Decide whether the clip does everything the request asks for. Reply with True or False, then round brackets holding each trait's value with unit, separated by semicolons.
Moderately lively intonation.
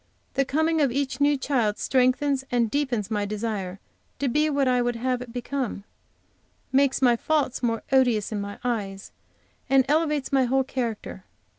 True (3.4 semitones)